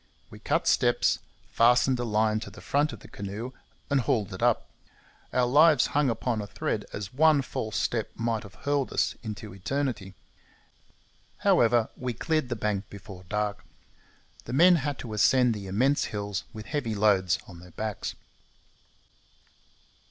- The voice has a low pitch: Yes, low, 115 Hz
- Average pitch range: Yes, average, 4.0 semitones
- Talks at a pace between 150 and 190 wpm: Yes, average, 160 wpm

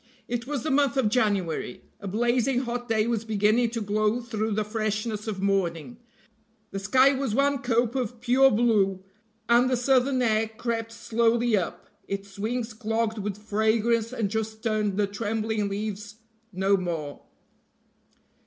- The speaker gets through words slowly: No, average, 155 wpm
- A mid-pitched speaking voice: No, high, 220 Hz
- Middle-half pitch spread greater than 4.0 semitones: No, narrow, 2.6 semitones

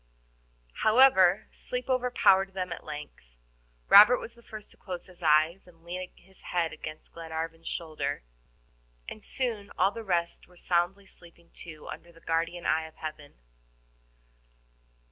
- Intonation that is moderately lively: Yes, average, 3.4 semitones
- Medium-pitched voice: Yes, medium, 175 Hz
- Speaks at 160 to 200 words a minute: No, average, 145 wpm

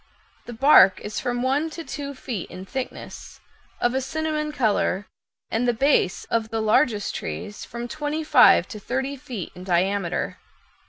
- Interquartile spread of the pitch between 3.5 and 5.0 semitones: No, wide, 5.5 semitones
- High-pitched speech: Yes, high, 240 Hz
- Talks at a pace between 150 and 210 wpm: Yes, average, 160 wpm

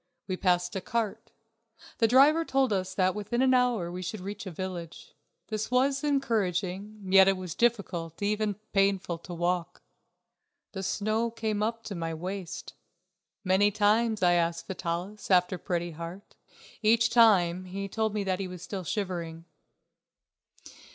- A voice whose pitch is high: Yes, high, 195 Hz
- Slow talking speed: No, average, 150 wpm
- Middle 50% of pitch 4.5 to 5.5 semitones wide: No, average, 3.4 semitones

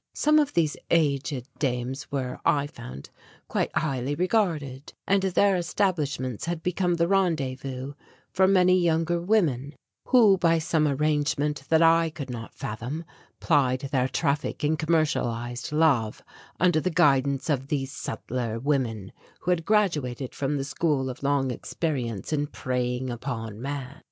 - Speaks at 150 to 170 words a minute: No, average, 140 wpm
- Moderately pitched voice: Yes, medium, 145 Hz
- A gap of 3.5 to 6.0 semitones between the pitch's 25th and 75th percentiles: Yes, average, 4.4 semitones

